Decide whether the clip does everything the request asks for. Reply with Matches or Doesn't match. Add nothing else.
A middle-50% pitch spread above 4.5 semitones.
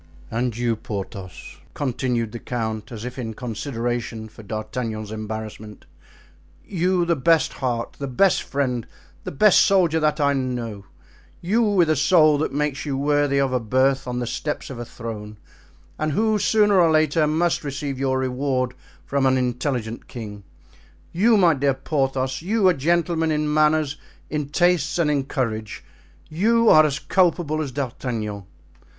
Matches